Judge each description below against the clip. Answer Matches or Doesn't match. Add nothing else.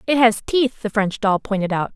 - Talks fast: Matches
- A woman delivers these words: Matches